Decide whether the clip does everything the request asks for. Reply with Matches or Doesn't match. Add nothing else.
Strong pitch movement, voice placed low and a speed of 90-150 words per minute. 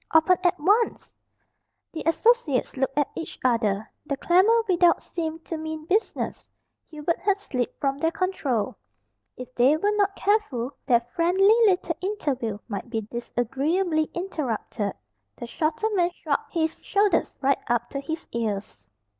Doesn't match